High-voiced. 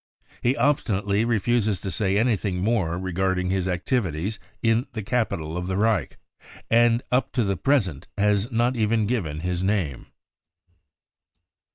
No: low, 105 Hz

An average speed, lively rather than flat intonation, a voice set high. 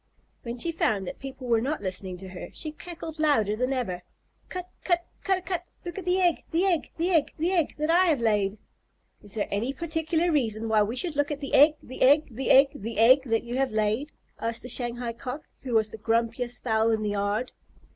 No: fast, 225 wpm; wide, 6.1 semitones; very high, 255 Hz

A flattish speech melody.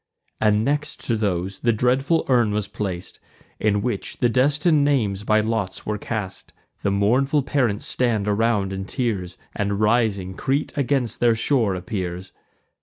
No: average, 3.9 semitones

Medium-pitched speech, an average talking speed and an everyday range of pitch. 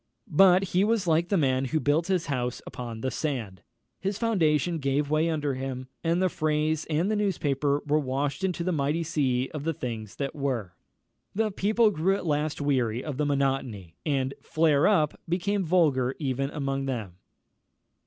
Yes: medium, 150 Hz; average, 175 wpm; average, 4.2 semitones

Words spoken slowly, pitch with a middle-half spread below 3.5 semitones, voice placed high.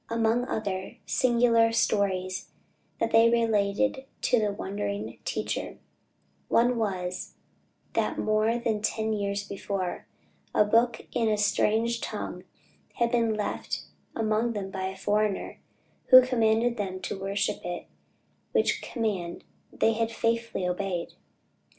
Yes: slow, 125 wpm; average, 2.8 semitones; high, 215 Hz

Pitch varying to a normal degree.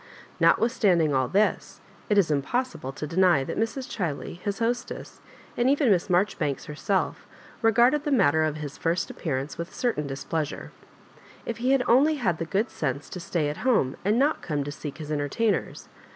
No: wide, 7.7 semitones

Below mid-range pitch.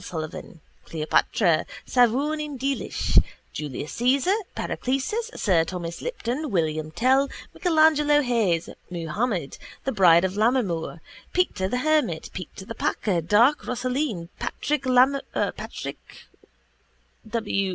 No: high, 230 Hz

